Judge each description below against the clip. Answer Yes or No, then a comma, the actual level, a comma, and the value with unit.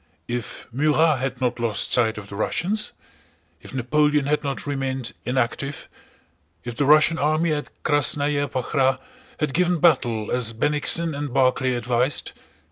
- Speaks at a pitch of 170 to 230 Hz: No, low, 135 Hz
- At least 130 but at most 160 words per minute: Yes, average, 140 wpm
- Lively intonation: No, average, 3.4 semitones